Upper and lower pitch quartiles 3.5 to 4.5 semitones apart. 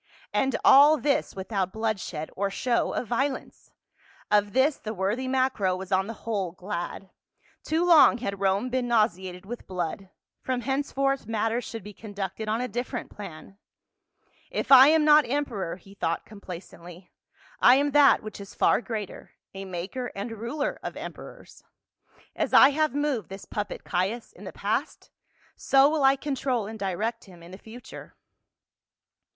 No: wide, 5.4 semitones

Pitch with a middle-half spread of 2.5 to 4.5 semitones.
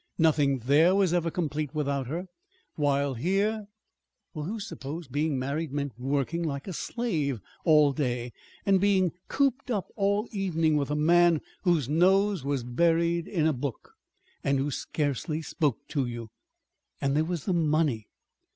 Yes: average, 4.0 semitones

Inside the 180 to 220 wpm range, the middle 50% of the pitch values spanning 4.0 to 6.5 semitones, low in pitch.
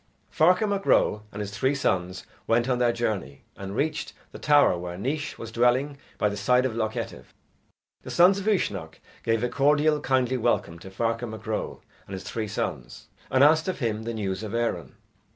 Yes: average, 195 wpm; wide, 5.5 semitones; low, 115 Hz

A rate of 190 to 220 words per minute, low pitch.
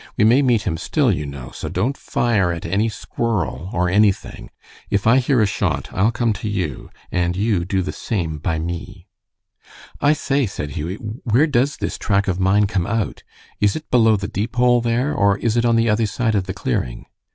Yes: fast, 205 wpm; low, 105 Hz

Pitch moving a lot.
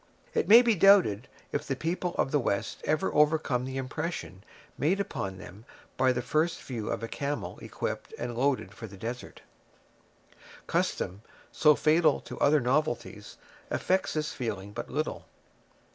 Yes: wide, 5.7 semitones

